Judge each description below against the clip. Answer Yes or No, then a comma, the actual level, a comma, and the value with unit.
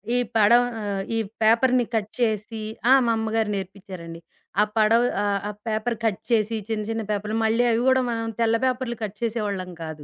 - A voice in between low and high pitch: No, high, 220 Hz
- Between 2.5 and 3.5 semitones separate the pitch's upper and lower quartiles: No, narrow, 2.1 semitones